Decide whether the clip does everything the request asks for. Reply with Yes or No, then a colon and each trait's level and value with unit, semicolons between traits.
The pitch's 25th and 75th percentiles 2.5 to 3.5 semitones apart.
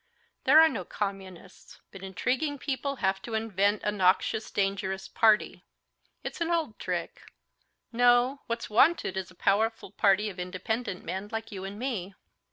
No: average, 4.1 semitones